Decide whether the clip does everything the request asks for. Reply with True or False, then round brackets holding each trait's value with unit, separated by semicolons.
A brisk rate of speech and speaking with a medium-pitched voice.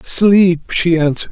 False (135 wpm; 175 Hz)